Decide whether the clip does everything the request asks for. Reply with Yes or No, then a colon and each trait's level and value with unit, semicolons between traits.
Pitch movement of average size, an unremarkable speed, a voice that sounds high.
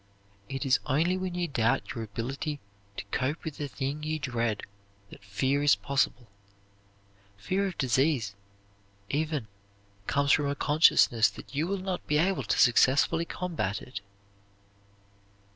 No: average, 4.1 semitones; average, 145 wpm; medium, 140 Hz